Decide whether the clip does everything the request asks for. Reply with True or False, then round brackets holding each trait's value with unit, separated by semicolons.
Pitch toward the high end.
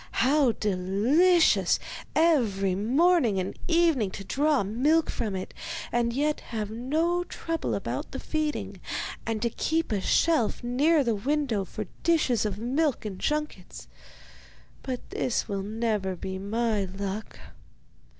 True (235 Hz)